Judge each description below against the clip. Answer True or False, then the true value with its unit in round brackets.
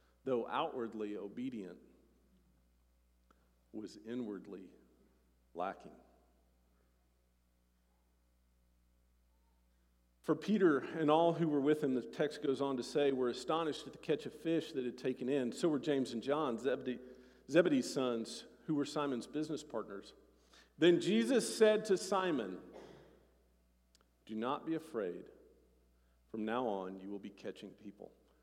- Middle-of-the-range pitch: False (120 Hz)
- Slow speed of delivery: True (130 wpm)